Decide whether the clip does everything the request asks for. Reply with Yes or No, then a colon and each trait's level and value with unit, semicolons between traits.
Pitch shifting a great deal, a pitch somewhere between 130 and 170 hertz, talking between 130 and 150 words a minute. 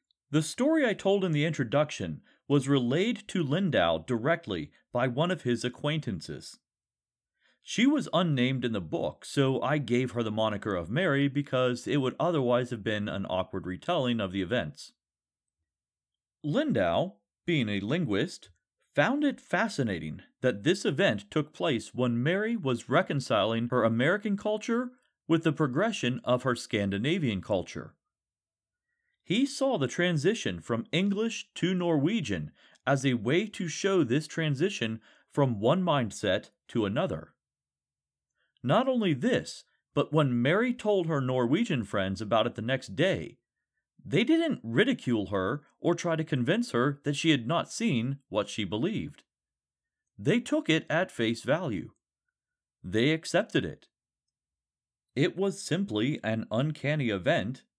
Yes: wide, 7.1 semitones; medium, 140 Hz; average, 140 wpm